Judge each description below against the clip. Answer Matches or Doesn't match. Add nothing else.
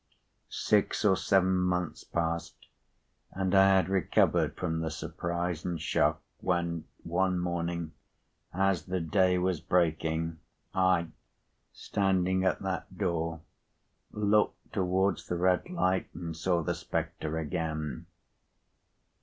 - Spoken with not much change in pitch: Matches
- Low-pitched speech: Matches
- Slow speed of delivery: Matches